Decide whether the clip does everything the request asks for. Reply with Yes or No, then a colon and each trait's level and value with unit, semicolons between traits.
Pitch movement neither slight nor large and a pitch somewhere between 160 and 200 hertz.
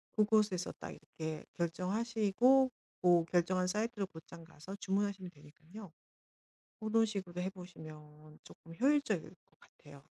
Yes: average, 4.6 semitones; medium, 185 Hz